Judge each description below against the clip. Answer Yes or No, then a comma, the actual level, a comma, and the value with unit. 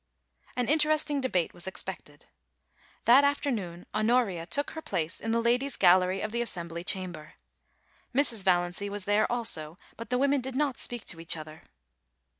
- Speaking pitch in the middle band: No, high, 215 Hz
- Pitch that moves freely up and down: Yes, wide, 6.3 semitones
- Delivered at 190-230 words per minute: No, average, 170 wpm